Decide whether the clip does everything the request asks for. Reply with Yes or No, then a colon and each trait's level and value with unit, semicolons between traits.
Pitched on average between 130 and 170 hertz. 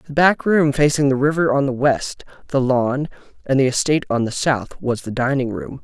Yes: low, 135 Hz